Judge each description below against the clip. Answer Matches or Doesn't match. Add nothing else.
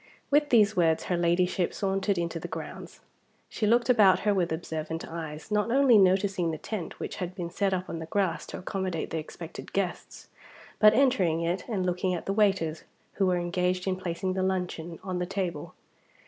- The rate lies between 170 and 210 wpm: Matches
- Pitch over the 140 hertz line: Matches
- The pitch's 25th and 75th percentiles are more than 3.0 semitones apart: Doesn't match